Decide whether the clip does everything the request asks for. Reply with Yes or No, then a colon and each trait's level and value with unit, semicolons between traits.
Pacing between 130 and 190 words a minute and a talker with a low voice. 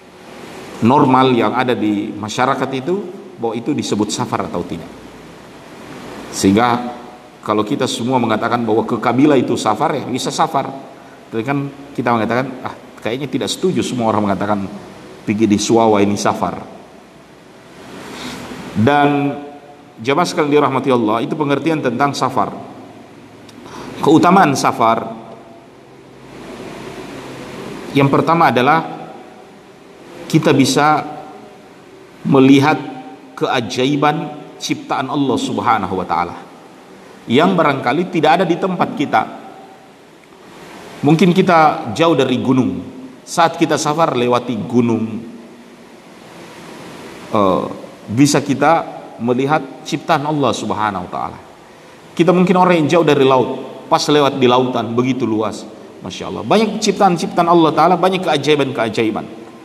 No: average, 110 wpm; low, 130 Hz